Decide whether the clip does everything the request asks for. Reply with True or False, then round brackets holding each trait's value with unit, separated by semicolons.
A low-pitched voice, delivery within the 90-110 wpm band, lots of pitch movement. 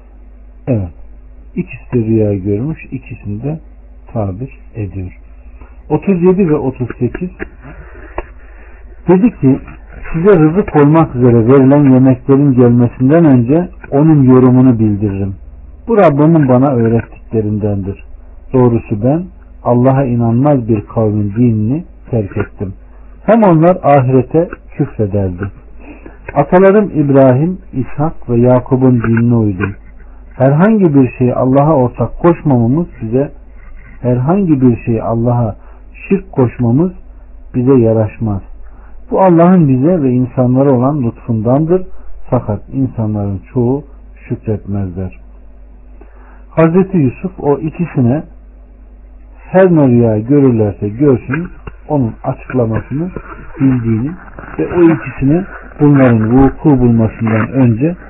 True (125 Hz; 95 wpm; 5.7 semitones)